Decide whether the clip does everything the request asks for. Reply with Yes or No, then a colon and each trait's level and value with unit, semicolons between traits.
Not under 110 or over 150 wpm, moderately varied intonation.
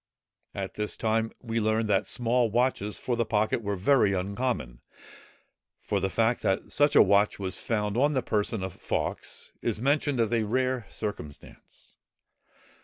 No: average, 160 wpm; average, 3.1 semitones